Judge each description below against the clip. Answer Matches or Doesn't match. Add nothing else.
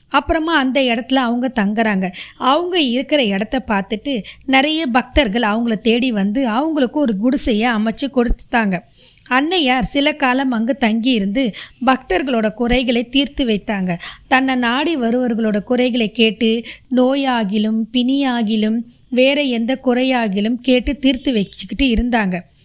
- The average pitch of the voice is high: Matches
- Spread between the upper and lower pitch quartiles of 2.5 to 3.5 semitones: Matches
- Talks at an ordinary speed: Matches